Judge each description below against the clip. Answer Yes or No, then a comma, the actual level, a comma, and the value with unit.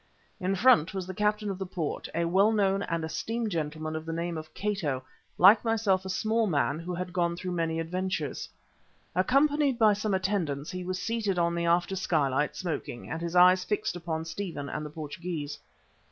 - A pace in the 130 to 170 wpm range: No, average, 190 wpm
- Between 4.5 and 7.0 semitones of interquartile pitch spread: No, average, 3.5 semitones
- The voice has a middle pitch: Yes, medium, 180 Hz